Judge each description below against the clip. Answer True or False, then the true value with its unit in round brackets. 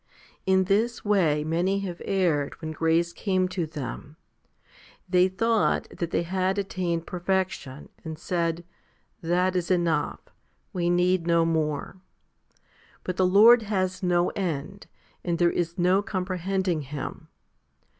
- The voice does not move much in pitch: True (2.3 semitones)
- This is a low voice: False (180 Hz)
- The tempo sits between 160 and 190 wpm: False (135 wpm)